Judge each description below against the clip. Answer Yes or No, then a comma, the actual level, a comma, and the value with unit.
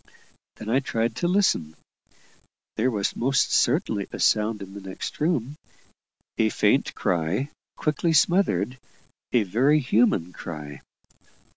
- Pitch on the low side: Yes, low, 115 Hz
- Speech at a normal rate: No, slow, 125 wpm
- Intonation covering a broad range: Yes, wide, 6.5 semitones